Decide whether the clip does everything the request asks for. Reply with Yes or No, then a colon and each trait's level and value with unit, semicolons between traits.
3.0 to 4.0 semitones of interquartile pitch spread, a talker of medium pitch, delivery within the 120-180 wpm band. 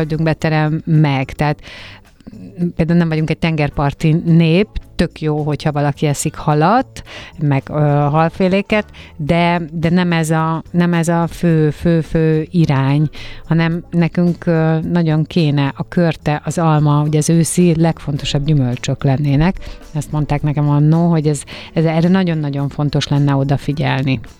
No: narrow, 2.4 semitones; medium, 155 Hz; average, 145 wpm